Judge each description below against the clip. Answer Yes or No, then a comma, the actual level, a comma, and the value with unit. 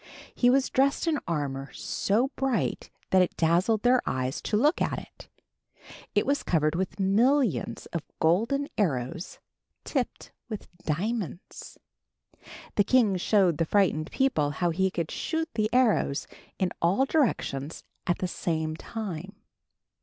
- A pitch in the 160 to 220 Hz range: Yes, high, 190 Hz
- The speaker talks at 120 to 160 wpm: Yes, average, 140 wpm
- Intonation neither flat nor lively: No, wide, 7.0 semitones